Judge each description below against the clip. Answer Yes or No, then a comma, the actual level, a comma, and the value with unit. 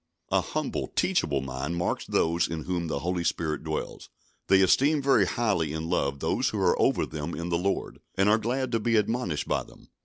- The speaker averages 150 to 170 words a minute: No, fast, 205 wpm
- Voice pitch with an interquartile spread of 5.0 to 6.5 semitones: Yes, wide, 5.6 semitones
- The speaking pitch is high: No, very low, 85 Hz